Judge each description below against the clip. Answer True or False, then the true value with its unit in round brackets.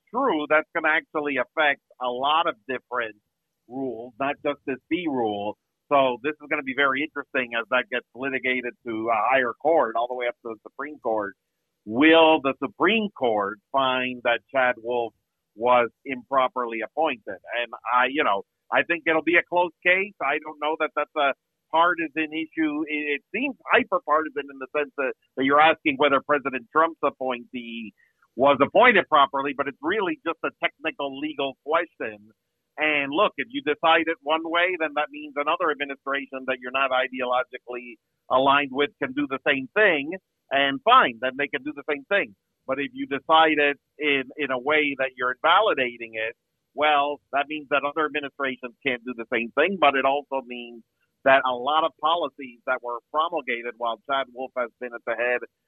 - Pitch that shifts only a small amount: False (3.5 semitones)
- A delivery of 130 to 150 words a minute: False (185 wpm)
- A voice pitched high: False (140 Hz)